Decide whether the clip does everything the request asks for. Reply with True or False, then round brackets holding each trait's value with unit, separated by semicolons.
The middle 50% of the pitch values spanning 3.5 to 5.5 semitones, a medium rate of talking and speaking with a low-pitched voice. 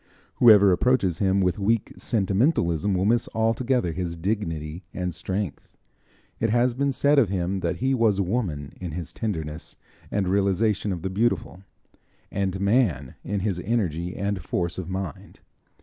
True (4.1 semitones; 150 wpm; 95 Hz)